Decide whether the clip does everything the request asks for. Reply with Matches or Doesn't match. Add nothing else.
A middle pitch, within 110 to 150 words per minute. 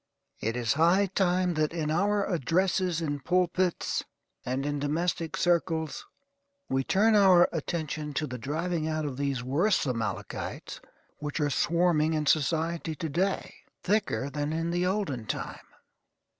Matches